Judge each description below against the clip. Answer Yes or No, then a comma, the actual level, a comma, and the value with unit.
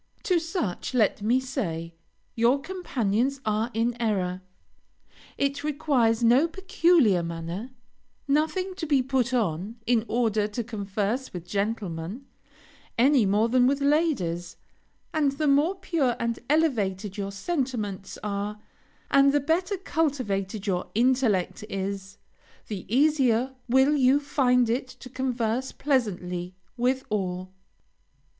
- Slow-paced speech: Yes, slow, 125 wpm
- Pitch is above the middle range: Yes, high, 240 Hz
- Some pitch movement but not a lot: No, wide, 5.7 semitones